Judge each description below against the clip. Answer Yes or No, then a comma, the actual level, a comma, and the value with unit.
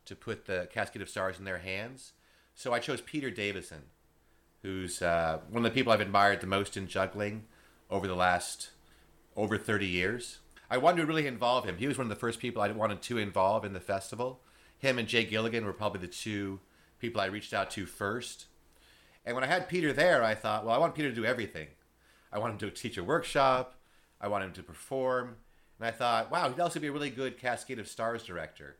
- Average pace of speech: No, fast, 225 wpm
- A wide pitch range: No, average, 4.8 semitones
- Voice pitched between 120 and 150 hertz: No, low, 110 Hz